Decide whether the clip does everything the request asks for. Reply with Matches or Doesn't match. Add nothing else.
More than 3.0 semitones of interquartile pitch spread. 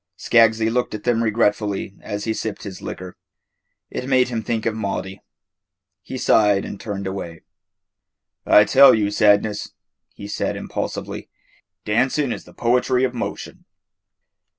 Doesn't match